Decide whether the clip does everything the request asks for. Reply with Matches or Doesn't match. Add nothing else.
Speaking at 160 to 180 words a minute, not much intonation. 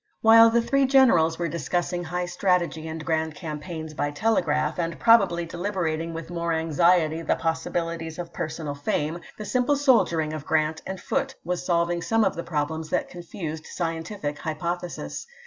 Matches